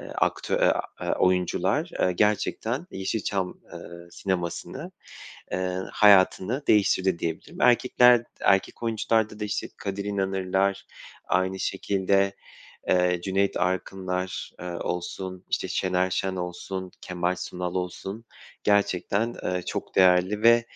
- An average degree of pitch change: No, narrow, 2.1 semitones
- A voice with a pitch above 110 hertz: No, very low, 95 Hz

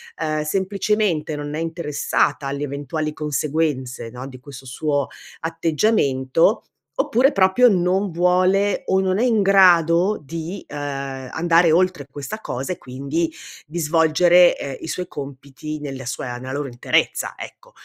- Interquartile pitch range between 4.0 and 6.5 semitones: Yes, average, 4.6 semitones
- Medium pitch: Yes, medium, 160 Hz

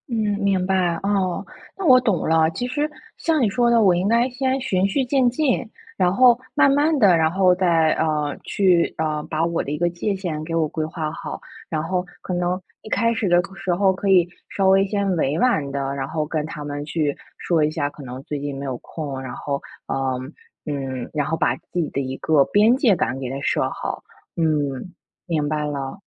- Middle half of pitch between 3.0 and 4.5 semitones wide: No, average, 5.2 semitones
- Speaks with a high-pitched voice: No, medium, 175 Hz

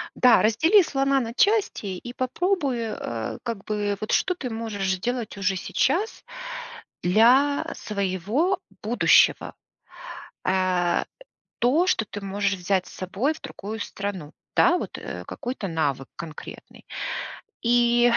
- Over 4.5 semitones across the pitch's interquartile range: Yes, wide, 5.4 semitones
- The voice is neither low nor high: No, high, 225 Hz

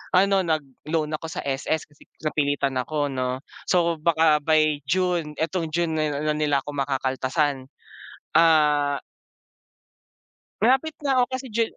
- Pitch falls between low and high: Yes, medium, 155 Hz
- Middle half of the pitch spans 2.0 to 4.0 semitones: Yes, average, 3.0 semitones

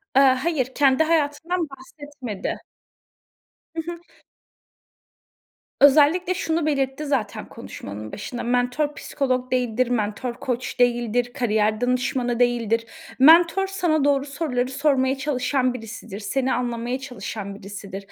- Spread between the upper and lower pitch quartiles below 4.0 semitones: Yes, average, 3.3 semitones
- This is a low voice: No, very high, 255 Hz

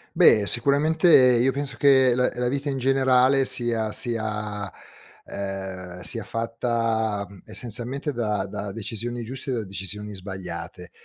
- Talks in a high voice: No, low, 115 Hz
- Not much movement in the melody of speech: No, average, 4.0 semitones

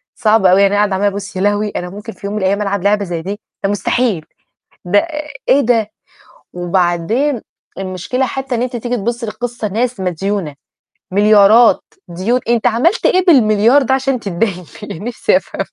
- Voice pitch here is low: No, high, 210 Hz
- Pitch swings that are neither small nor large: Yes, average, 3.8 semitones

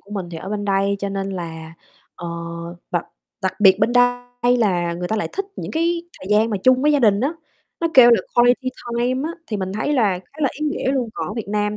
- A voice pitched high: Yes, high, 215 Hz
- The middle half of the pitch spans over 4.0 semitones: Yes, average, 4.4 semitones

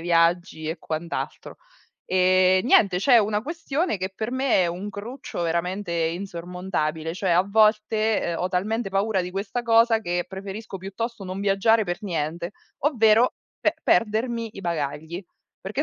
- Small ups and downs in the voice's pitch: No, average, 3.9 semitones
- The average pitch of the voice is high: Yes, high, 195 Hz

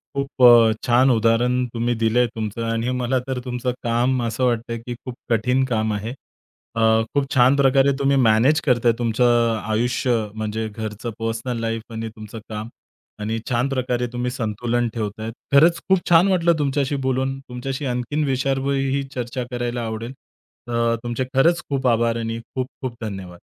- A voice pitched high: No, low, 120 Hz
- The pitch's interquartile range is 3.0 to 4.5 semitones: No, narrow, 2.6 semitones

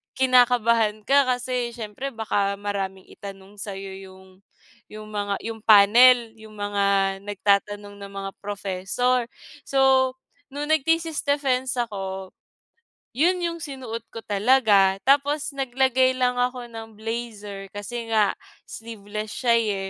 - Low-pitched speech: No, high, 225 Hz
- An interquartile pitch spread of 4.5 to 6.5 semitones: No, average, 4.1 semitones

